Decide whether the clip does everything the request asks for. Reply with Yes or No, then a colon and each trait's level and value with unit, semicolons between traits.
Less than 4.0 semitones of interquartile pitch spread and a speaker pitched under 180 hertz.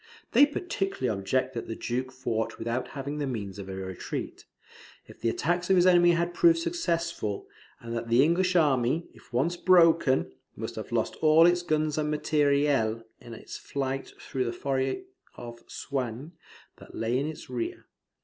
No: wide, 6.1 semitones; medium, 140 Hz